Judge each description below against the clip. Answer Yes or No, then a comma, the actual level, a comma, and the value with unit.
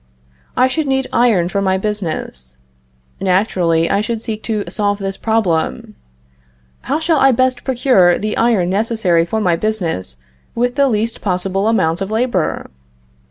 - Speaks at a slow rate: No, average, 150 wpm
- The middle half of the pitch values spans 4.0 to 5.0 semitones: Yes, average, 4.4 semitones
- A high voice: Yes, high, 210 Hz